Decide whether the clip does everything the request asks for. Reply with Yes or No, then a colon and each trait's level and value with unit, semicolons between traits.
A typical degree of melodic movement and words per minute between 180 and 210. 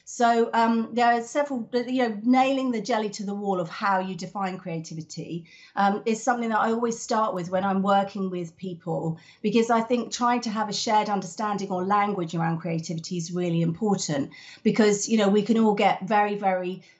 Yes: average, 3.9 semitones; average, 200 wpm